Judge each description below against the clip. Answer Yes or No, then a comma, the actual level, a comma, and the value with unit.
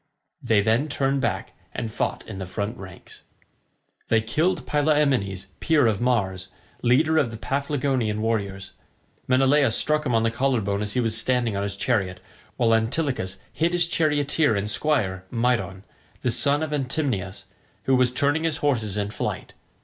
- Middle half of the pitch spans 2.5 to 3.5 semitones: No, wide, 5.5 semitones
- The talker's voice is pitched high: No, low, 120 Hz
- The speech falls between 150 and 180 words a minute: Yes, average, 165 wpm